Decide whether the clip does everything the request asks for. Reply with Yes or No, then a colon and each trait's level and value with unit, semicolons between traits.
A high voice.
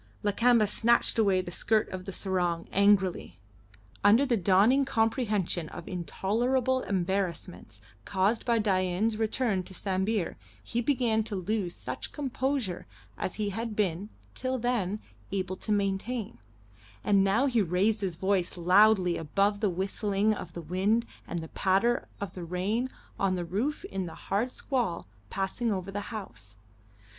Yes: high, 200 Hz